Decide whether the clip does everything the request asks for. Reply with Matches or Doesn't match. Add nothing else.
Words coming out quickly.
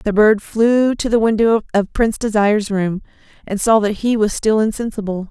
Doesn't match